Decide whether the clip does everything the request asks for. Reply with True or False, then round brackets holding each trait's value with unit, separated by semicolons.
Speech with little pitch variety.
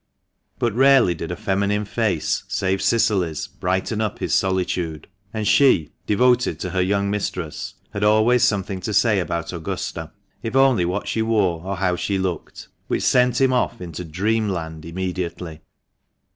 False (3.6 semitones)